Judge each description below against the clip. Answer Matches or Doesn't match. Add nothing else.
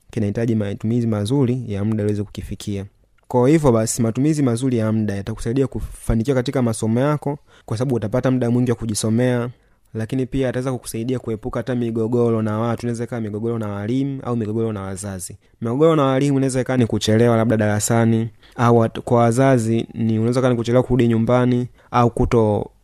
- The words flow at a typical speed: Doesn't match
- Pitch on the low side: Matches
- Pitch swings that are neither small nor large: Doesn't match